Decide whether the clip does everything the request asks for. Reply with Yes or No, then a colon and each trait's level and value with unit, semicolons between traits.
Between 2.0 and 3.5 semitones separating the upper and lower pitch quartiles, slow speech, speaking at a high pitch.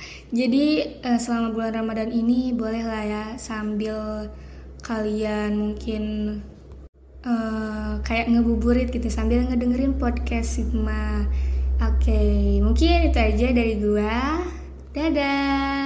No: narrow, 2.5 semitones; average, 100 wpm; high, 225 Hz